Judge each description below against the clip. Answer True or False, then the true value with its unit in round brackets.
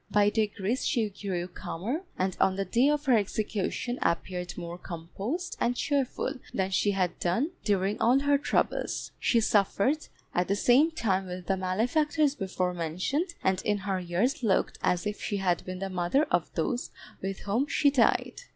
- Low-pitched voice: False (205 Hz)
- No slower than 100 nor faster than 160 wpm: False (175 wpm)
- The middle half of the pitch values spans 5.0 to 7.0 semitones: True (5.4 semitones)